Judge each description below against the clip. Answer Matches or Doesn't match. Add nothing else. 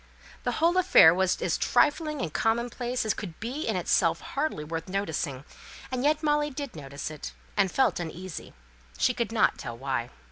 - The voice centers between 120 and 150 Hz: Doesn't match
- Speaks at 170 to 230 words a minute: Matches